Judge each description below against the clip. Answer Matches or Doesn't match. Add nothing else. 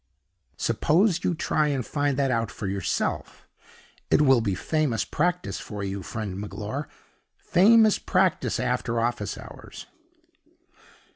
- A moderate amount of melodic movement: Doesn't match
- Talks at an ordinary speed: Doesn't match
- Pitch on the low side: Matches